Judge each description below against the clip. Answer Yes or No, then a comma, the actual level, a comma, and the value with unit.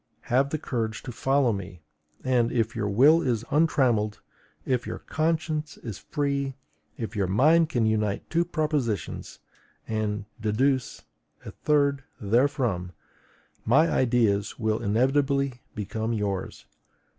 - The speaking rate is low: Yes, slow, 120 wpm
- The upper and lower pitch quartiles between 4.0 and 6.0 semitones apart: Yes, average, 4.7 semitones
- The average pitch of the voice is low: Yes, low, 120 Hz